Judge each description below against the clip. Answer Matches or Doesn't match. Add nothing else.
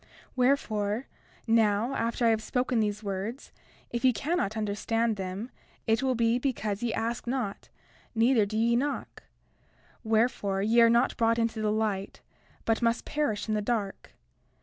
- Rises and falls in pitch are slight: Matches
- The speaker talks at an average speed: Matches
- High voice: Matches